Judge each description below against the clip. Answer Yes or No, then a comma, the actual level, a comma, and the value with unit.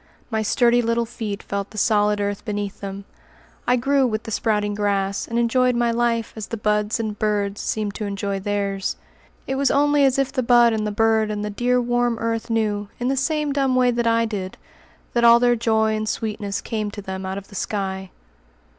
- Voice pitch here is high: Yes, high, 220 Hz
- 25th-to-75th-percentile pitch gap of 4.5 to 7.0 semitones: No, average, 2.7 semitones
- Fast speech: Yes, fast, 210 wpm